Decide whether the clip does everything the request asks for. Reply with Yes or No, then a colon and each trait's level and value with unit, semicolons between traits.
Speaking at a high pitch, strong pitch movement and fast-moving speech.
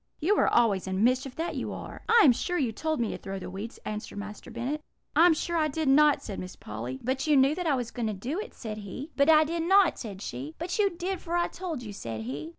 Yes: very high, 265 Hz; wide, 7.9 semitones; fast, 270 wpm